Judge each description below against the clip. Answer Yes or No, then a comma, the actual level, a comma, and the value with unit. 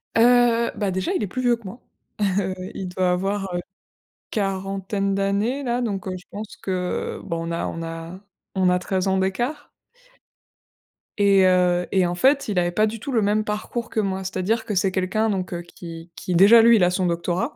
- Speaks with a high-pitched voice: Yes, high, 195 Hz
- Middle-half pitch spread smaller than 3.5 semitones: Yes, average, 3.1 semitones